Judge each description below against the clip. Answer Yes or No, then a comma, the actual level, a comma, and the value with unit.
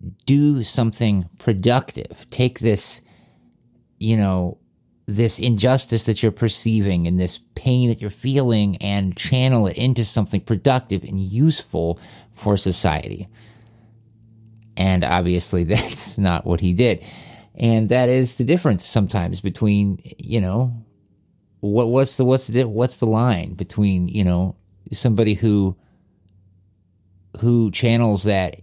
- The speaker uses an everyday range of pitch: Yes, average, 3.9 semitones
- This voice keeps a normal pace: No, slow, 125 wpm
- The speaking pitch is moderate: No, low, 105 Hz